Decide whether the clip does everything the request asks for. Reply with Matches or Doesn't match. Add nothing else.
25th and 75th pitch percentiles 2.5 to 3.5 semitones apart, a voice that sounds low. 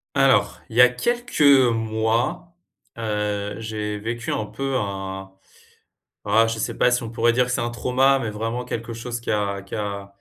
Matches